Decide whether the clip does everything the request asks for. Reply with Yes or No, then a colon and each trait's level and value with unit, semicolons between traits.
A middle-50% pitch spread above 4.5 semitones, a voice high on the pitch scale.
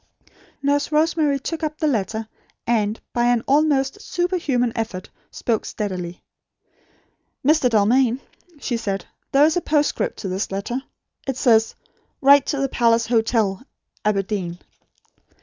Yes: average, 5.0 semitones; high, 240 Hz